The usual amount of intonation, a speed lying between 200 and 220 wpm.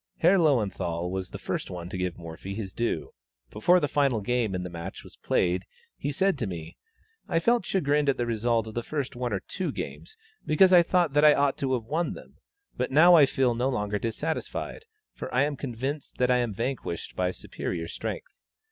No: wide, 7.2 semitones; fast, 205 wpm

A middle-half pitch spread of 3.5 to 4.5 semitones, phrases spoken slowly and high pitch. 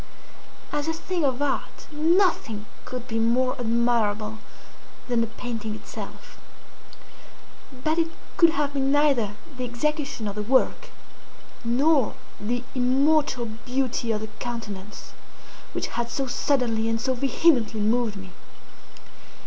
Yes: average, 3.9 semitones; slow, 125 wpm; high, 245 Hz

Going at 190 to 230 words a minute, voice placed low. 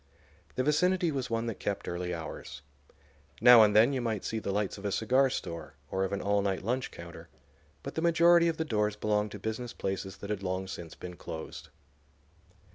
Yes: average, 200 wpm; low, 105 Hz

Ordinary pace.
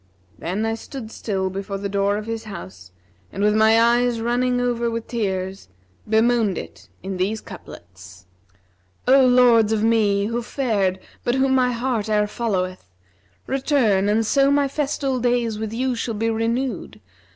Yes: average, 160 wpm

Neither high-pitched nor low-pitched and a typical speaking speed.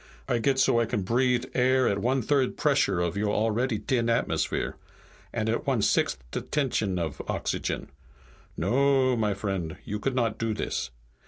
No: low, 115 Hz; average, 175 wpm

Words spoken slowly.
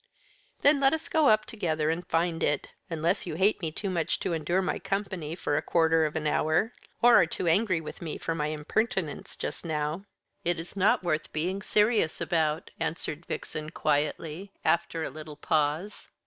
No: average, 185 wpm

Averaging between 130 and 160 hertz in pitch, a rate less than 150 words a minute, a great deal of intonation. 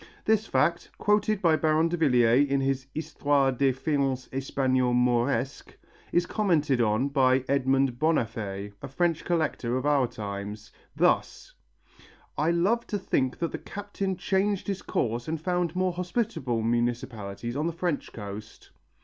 Yes: medium, 140 Hz; average, 140 wpm; wide, 5.9 semitones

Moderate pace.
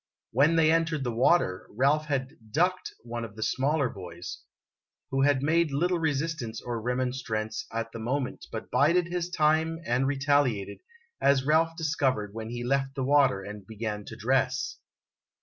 Yes: average, 160 wpm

